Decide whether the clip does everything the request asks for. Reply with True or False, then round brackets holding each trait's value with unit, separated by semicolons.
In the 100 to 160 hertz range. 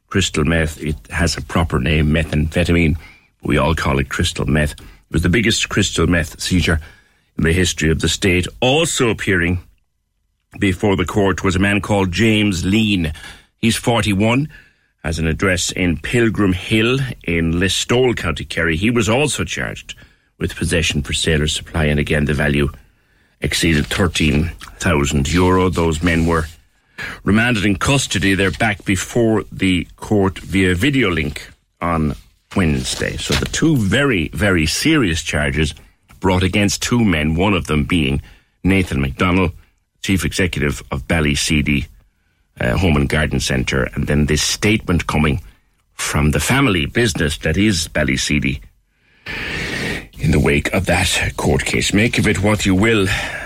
False (85 Hz)